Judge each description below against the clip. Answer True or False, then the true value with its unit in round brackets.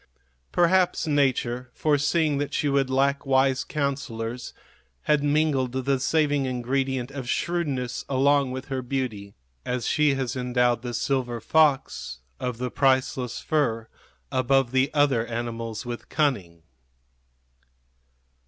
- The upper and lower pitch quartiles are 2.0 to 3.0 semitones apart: True (2.6 semitones)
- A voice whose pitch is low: True (130 Hz)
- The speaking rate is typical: False (120 wpm)